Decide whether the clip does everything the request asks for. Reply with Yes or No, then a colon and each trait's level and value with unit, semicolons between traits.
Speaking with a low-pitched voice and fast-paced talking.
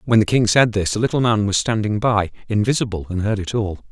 Yes: low, 105 Hz; fast, 245 wpm